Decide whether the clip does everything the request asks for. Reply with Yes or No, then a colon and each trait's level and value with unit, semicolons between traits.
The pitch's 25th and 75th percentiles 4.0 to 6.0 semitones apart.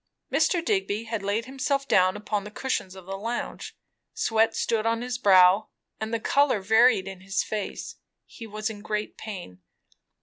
No: average, 3.0 semitones